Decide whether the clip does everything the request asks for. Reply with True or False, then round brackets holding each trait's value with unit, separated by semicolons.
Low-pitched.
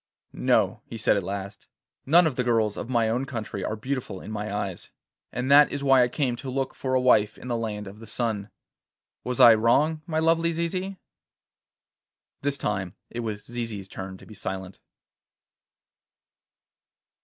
True (115 Hz)